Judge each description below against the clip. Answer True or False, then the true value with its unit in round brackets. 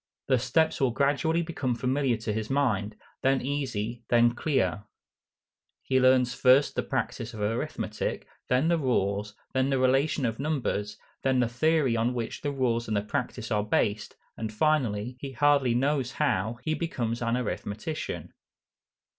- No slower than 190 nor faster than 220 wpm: False (155 wpm)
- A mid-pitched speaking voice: False (125 Hz)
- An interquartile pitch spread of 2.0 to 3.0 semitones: False (3.6 semitones)